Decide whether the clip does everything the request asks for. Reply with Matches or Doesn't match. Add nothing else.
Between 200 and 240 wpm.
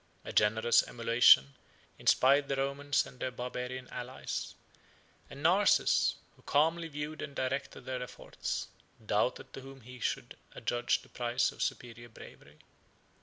Doesn't match